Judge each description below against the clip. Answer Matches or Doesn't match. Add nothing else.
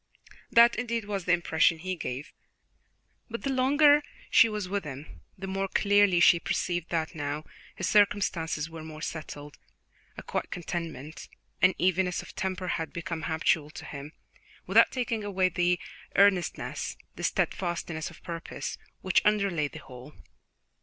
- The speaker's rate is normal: Matches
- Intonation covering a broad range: Doesn't match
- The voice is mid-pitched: Matches